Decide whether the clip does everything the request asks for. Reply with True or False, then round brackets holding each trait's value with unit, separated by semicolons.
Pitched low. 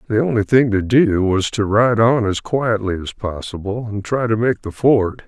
True (110 Hz)